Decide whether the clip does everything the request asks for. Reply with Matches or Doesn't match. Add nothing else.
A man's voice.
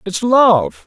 Matches